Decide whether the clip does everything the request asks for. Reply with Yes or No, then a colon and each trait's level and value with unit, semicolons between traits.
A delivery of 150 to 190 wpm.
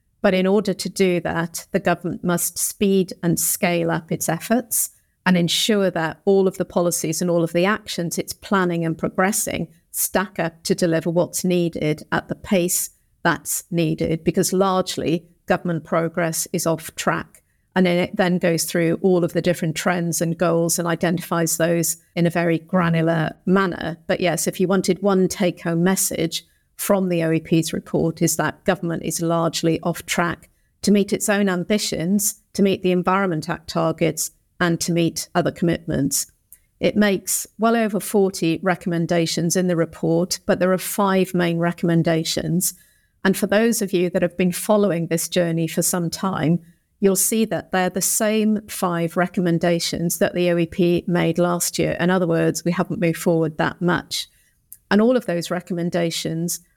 Yes: average, 170 wpm